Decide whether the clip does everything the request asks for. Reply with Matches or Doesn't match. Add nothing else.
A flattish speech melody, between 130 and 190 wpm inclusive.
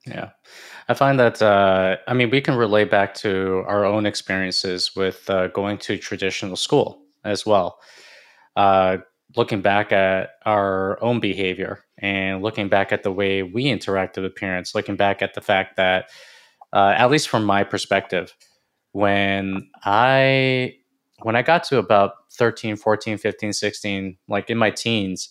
Matches